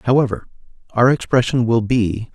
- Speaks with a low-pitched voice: Yes, low, 120 Hz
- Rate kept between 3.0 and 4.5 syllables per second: No, 5.1 syllables/s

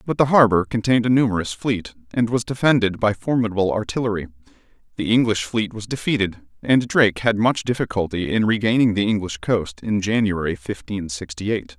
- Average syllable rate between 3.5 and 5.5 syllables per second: No, 5.7 syllables/s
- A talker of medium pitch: No, low, 105 Hz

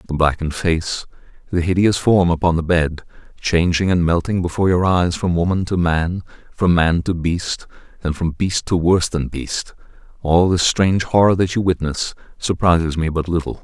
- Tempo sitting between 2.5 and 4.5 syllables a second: No, 5.1 syllables/s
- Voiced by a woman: No, male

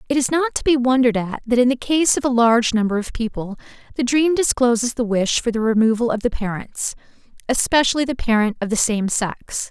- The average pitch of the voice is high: Yes, high, 240 Hz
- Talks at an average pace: No, fast, 215 wpm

